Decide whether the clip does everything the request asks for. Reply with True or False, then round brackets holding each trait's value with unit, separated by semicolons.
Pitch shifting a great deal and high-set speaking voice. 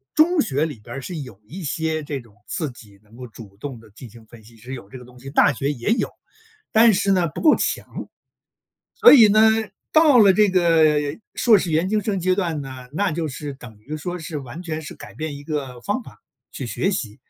False (6.8 semitones; 150 Hz)